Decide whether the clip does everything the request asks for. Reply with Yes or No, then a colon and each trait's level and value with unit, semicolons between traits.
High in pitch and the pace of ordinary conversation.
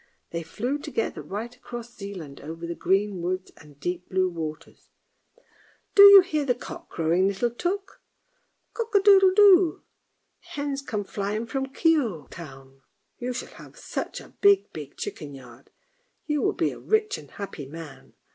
Yes: high, 210 Hz; average, 170 wpm